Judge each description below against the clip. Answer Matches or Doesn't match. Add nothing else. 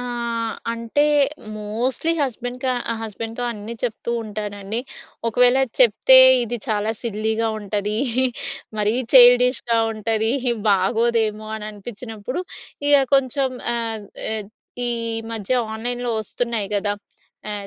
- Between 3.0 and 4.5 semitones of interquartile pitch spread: Doesn't match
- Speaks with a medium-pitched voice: Doesn't match